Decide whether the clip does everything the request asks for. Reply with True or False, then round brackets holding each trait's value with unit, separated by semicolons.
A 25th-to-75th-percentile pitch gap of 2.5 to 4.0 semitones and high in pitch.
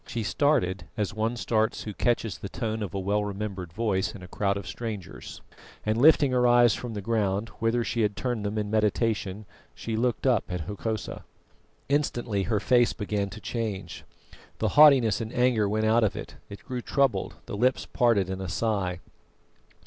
False (3.0 semitones; 110 Hz)